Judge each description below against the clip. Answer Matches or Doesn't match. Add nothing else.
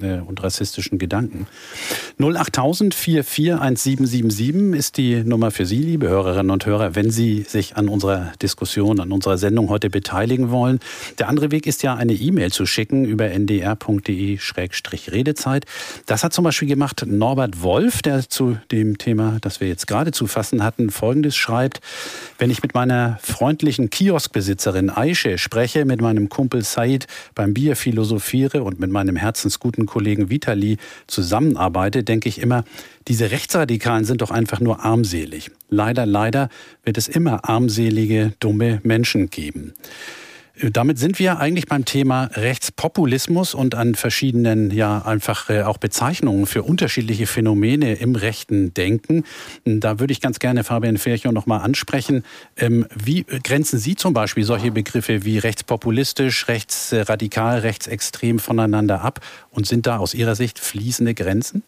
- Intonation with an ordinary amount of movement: Matches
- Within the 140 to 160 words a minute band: Matches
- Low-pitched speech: Matches